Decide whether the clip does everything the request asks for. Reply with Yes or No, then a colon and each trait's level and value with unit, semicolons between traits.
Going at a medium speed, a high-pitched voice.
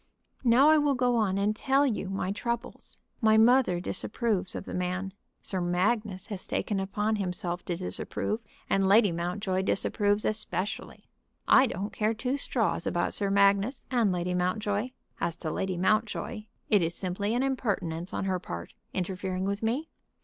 Yes: average, 165 wpm; high, 200 Hz